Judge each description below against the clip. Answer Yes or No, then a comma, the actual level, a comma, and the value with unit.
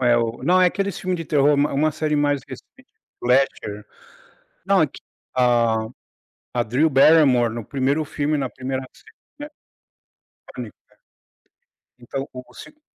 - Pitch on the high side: No, medium, 140 Hz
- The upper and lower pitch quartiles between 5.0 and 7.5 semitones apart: No, average, 4.1 semitones